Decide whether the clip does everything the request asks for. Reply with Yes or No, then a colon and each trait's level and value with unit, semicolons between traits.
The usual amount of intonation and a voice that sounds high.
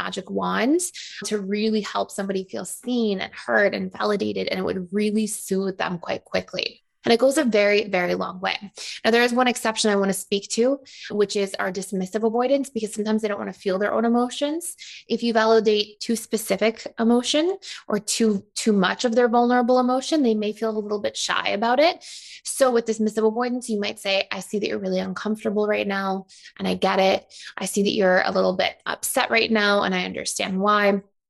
Yes: average, 3.4 semitones; high, 215 Hz